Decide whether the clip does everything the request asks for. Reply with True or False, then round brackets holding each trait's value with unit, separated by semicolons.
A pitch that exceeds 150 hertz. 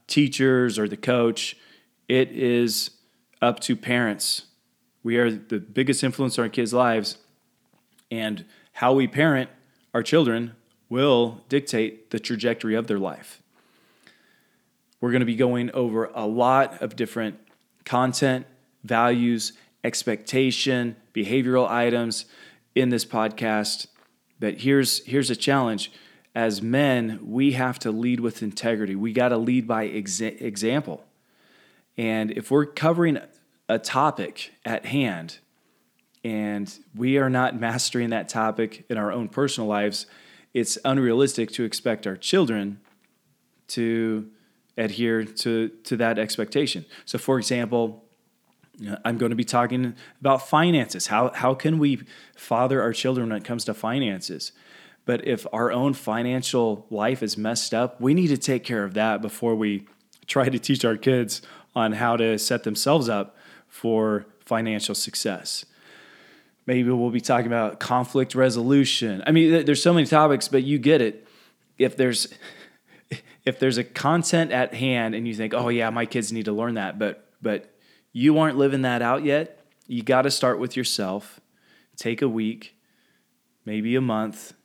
False (120 Hz)